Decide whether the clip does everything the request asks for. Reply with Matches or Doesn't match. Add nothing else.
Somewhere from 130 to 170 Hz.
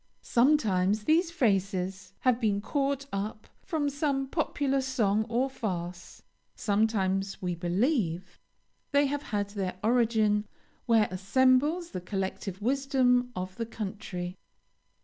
Doesn't match